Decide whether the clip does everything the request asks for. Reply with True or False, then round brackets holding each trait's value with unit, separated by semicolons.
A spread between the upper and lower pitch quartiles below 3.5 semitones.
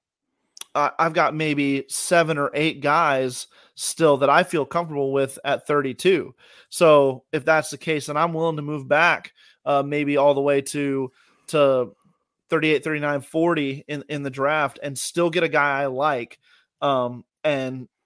True (2.5 semitones)